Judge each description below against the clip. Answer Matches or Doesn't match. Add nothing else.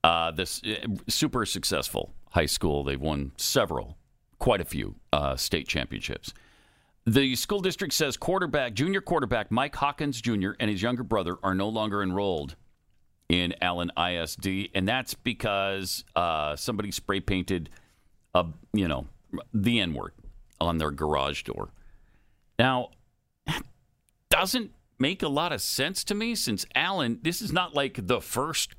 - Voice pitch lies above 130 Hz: Doesn't match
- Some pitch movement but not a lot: Doesn't match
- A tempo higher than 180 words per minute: Doesn't match